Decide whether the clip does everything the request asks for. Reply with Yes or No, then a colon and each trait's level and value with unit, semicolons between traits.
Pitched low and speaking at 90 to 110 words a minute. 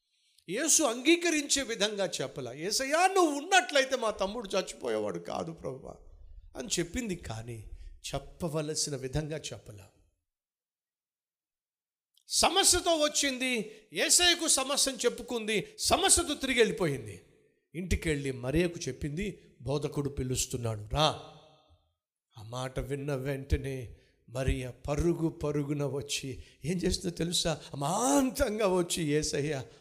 No: medium, 155 Hz; average, 95 wpm